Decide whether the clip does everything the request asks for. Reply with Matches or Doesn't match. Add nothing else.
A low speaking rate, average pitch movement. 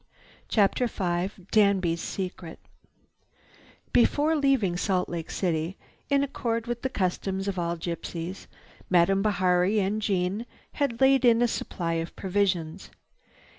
Matches